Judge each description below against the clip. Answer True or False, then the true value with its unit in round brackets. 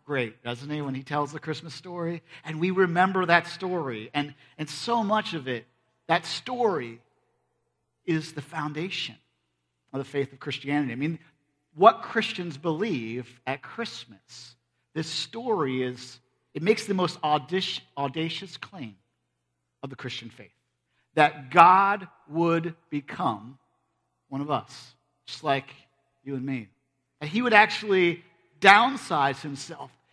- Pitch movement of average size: True (4.9 semitones)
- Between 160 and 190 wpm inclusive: False (135 wpm)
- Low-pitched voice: False (150 Hz)